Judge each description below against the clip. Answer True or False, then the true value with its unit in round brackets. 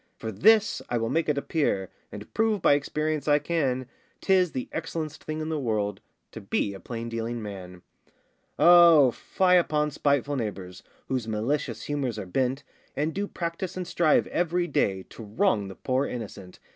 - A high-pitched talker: False (140 Hz)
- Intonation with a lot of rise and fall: True (6.5 semitones)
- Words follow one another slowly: False (170 wpm)